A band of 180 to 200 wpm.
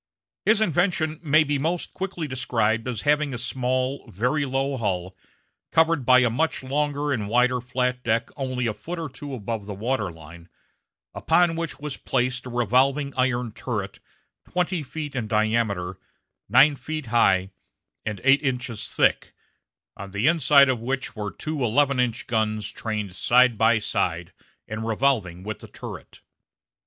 No: average, 155 wpm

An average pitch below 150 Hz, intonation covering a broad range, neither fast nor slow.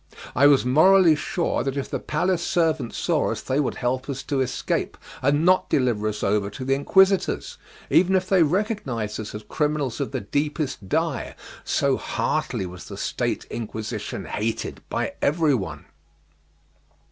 Yes: medium, 140 Hz; wide, 5.8 semitones; average, 160 wpm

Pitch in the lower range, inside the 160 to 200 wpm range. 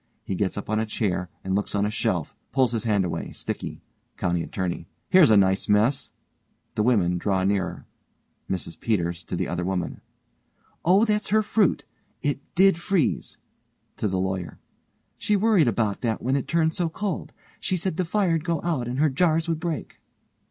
Yes: low, 120 Hz; average, 180 wpm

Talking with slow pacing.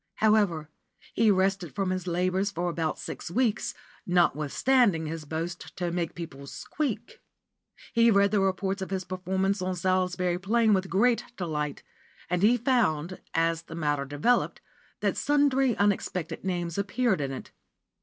No: average, 145 wpm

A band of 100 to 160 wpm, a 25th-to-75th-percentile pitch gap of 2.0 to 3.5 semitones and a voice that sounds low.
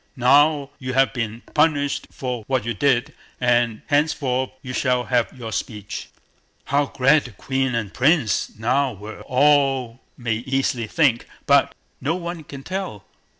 Yes: average, 150 wpm; average, 3.1 semitones; low, 130 Hz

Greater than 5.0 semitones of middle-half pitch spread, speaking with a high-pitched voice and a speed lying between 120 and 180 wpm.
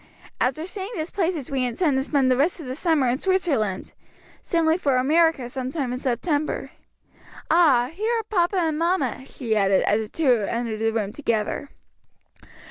Yes: wide, 5.6 semitones; very high, 275 Hz; average, 175 wpm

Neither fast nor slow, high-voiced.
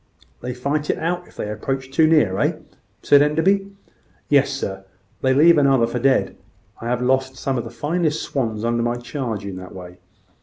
No: average, 195 wpm; low, 130 Hz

